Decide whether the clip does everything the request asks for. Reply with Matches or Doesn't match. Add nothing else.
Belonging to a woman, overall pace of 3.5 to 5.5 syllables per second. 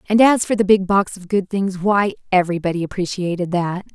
Doesn't match